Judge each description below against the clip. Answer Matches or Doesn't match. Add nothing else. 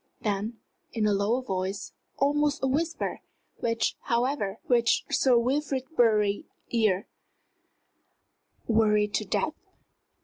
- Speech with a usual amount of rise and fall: Matches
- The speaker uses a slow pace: Matches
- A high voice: Matches